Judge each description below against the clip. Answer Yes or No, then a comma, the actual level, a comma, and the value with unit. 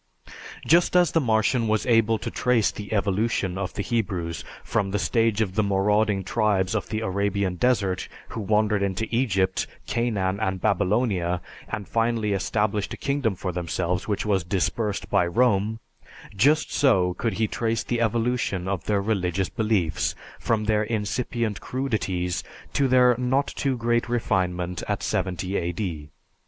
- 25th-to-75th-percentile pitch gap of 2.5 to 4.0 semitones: Yes, average, 3.5 semitones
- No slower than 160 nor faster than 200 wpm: No, average, 150 wpm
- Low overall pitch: Yes, low, 105 Hz